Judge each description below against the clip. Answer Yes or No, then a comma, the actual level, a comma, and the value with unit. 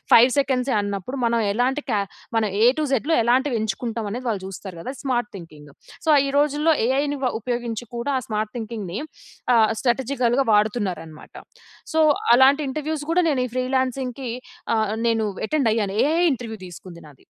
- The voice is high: Yes, high, 240 Hz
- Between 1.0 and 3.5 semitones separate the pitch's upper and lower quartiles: No, average, 3.9 semitones